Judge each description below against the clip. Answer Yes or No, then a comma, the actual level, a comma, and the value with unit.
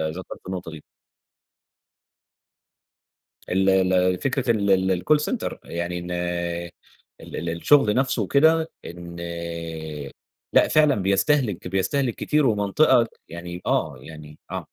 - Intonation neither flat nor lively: No, wide, 6.9 semitones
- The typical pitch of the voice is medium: No, very low, 95 Hz